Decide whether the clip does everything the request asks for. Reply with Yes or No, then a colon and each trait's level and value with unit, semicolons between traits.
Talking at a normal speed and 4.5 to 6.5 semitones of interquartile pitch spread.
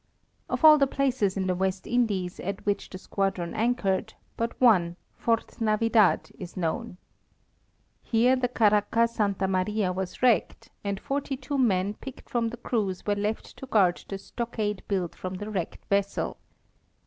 No: average, 160 wpm; average, 3.7 semitones